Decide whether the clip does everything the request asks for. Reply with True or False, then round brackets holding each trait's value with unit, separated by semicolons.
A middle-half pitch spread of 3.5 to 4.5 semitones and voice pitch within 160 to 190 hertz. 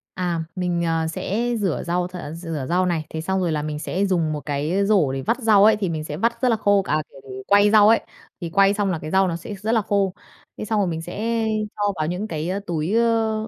True (4.2 semitones; 185 Hz)